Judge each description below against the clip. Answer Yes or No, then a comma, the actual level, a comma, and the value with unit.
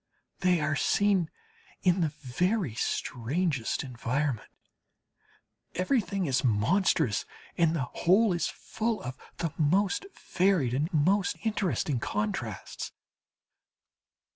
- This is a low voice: No, medium, 165 Hz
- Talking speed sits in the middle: No, slow, 100 wpm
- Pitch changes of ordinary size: No, wide, 6.7 semitones